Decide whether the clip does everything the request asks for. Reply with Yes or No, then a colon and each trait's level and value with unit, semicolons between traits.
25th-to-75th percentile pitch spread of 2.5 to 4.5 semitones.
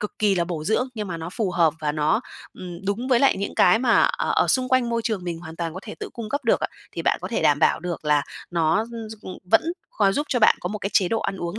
No: average, 5.0 semitones